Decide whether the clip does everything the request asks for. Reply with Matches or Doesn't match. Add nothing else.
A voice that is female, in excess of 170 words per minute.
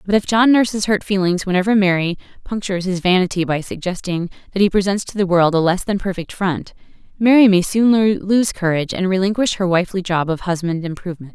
Matches